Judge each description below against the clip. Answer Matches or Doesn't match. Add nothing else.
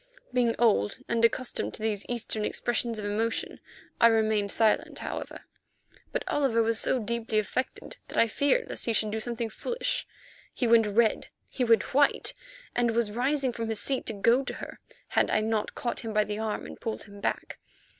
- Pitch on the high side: Matches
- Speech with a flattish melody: Matches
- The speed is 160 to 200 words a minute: Matches